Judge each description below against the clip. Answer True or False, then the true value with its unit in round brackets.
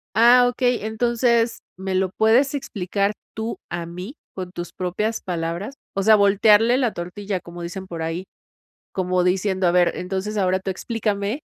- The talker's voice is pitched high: True (195 Hz)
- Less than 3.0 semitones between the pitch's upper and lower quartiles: False (3.8 semitones)